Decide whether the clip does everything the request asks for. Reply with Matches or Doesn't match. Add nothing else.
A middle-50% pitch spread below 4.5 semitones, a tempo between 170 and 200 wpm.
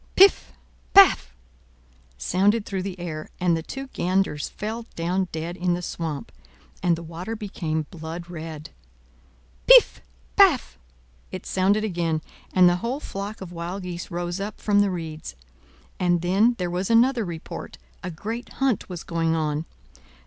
Doesn't match